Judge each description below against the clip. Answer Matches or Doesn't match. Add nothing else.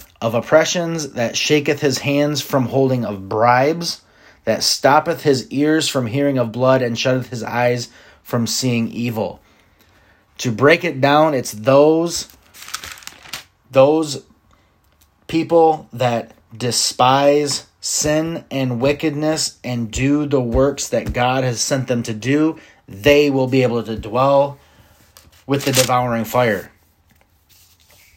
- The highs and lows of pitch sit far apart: Doesn't match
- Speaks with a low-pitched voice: Matches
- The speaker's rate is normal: Doesn't match